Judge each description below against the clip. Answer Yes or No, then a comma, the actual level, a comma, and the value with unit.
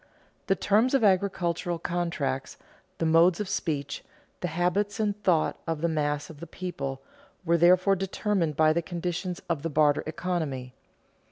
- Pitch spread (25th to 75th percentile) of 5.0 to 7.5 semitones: No, average, 2.9 semitones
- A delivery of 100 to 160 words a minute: Yes, average, 155 wpm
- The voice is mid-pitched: Yes, medium, 170 Hz